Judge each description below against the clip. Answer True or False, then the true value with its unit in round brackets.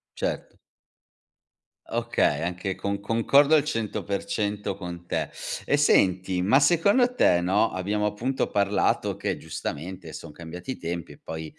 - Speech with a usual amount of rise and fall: True (4.7 semitones)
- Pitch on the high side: False (100 Hz)